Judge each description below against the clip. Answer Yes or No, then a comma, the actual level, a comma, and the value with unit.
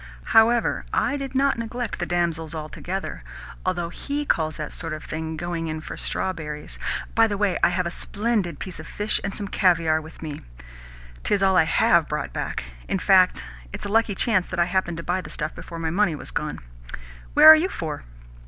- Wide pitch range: No, average, 4.6 semitones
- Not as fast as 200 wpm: No, fast, 205 wpm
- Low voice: No, medium, 175 Hz